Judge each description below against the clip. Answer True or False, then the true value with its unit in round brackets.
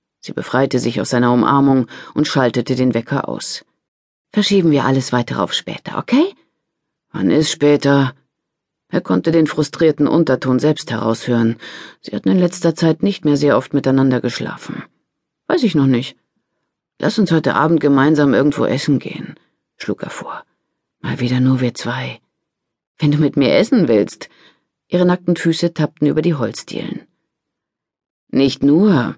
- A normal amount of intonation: True (3.9 semitones)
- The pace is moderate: True (150 wpm)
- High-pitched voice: False (140 Hz)